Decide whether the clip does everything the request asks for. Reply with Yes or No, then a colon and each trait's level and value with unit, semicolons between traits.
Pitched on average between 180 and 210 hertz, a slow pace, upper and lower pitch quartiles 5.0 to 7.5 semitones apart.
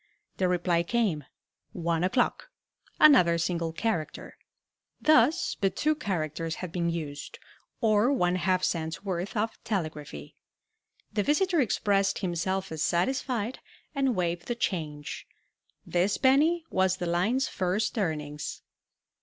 Yes: medium, 185 Hz; slow, 120 wpm; wide, 5.4 semitones